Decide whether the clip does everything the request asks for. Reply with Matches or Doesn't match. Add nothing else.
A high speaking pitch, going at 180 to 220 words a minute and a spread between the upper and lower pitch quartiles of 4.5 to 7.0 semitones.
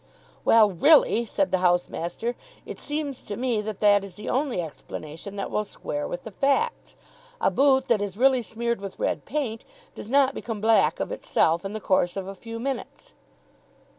Matches